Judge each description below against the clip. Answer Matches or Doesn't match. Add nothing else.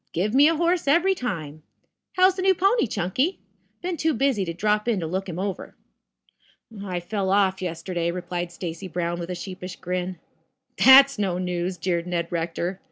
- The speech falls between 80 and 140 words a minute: Doesn't match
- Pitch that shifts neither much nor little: Doesn't match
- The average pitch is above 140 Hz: Matches